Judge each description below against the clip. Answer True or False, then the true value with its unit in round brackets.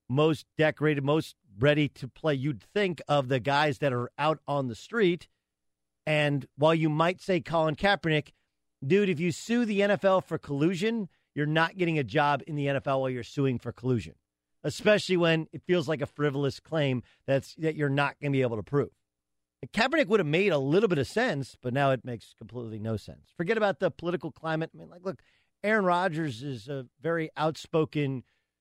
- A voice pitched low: False (150 Hz)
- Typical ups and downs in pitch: True (4.3 semitones)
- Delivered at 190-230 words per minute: True (195 wpm)